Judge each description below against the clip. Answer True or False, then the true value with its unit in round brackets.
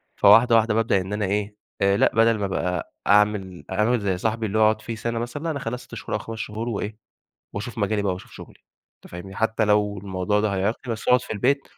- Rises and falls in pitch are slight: True (2.2 semitones)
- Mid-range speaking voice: False (105 Hz)